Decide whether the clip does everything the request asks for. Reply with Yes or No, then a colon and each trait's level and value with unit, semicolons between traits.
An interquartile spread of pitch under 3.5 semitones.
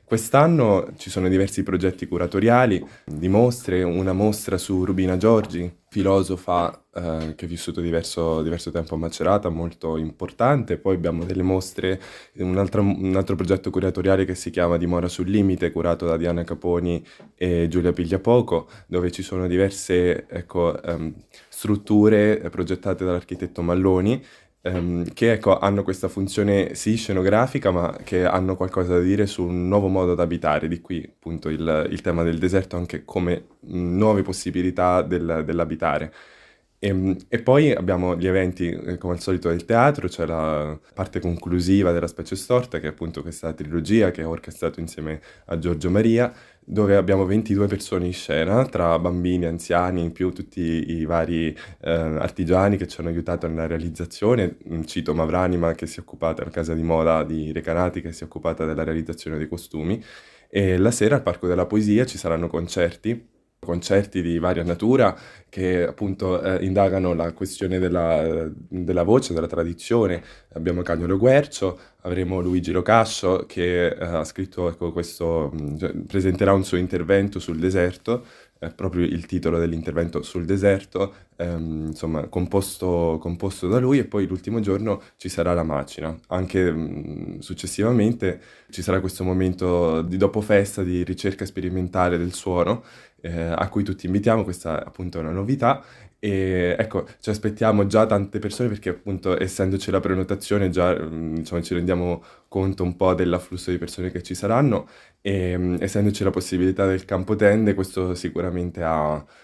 Yes: narrow, 2.4 semitones